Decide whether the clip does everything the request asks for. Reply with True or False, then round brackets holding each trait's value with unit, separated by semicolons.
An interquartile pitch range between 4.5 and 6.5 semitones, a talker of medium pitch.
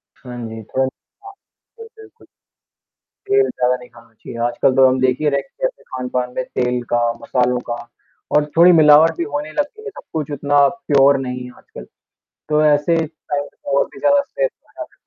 True (4.8 semitones; 145 Hz)